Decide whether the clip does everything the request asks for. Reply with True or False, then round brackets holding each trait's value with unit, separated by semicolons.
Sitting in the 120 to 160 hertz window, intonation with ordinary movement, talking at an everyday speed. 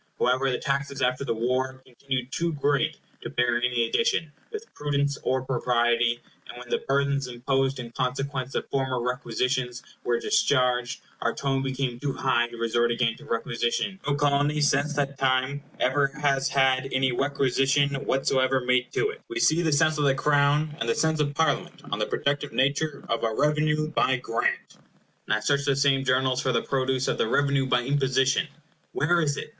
False (135 Hz; 2.3 semitones; 180 wpm)